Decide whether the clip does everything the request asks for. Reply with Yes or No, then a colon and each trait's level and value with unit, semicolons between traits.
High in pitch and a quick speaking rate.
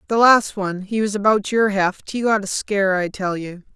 Yes: high, 200 Hz; fast, 210 wpm